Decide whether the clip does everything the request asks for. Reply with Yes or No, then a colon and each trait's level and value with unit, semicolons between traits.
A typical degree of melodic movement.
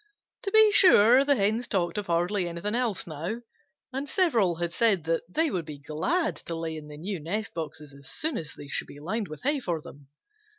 No: wide, 7.1 semitones